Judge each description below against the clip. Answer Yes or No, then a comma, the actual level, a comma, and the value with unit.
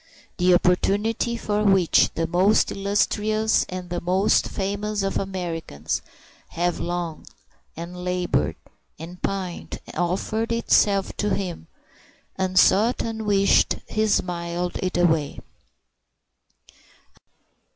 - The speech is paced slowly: Yes, slow, 100 wpm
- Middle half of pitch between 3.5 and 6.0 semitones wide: No, average, 2.8 semitones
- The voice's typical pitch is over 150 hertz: Yes, medium, 185 Hz